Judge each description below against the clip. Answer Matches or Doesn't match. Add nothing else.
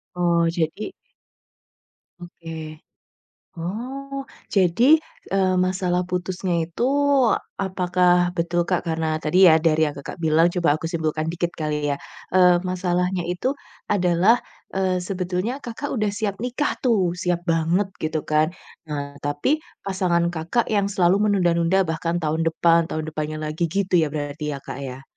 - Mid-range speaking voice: Matches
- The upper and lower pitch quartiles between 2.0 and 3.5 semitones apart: Matches